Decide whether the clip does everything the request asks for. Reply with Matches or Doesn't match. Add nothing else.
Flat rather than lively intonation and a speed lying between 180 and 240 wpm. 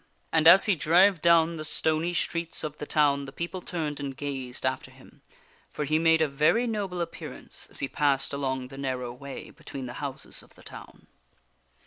Doesn't match